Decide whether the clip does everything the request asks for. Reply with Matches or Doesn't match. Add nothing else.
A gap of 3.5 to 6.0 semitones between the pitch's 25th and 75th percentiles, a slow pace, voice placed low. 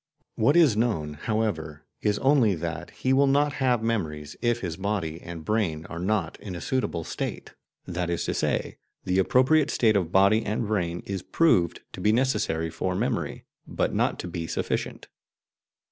Doesn't match